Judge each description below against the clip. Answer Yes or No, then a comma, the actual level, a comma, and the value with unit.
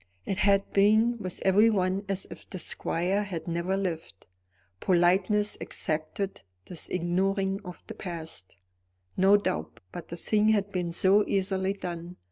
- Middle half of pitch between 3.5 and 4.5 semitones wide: No, narrow, 2.5 semitones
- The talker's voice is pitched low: No, high, 190 Hz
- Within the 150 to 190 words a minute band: No, average, 140 wpm